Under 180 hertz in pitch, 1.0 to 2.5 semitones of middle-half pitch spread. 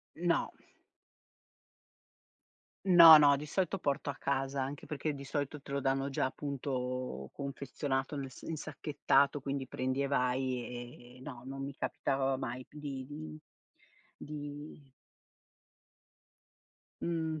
Yes: medium, 140 Hz; narrow, 1.9 semitones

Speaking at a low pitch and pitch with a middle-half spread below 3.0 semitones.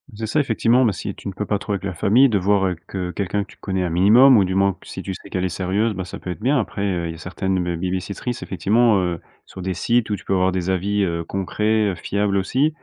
Yes: very low, 95 Hz; narrow, 2.6 semitones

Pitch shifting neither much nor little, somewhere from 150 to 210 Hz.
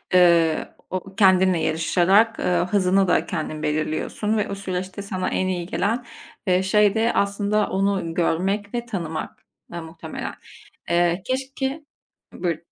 Yes: average, 3.0 semitones; medium, 185 Hz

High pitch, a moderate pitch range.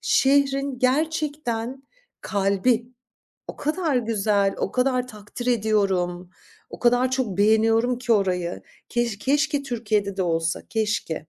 Yes: high, 230 Hz; average, 4.4 semitones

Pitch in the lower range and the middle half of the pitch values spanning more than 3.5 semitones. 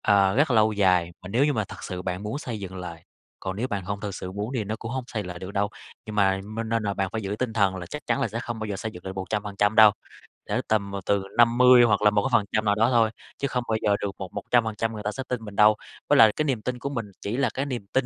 No: low, 105 Hz; average, 2.9 semitones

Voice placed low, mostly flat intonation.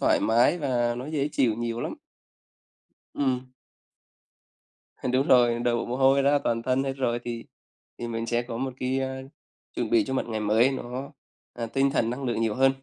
Yes: low, 125 Hz; narrow, 2.2 semitones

